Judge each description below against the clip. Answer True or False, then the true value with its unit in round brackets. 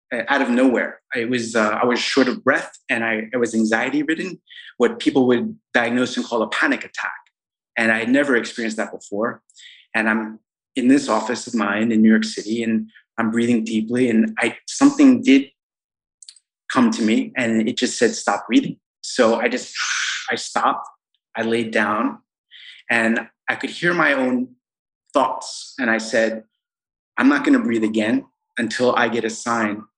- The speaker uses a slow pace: False (180 wpm)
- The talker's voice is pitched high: False (120 Hz)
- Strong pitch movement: True (7.7 semitones)